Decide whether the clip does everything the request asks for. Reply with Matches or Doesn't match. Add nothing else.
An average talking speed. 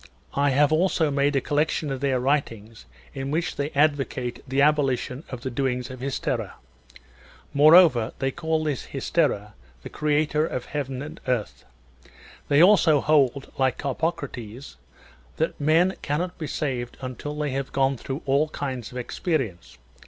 Matches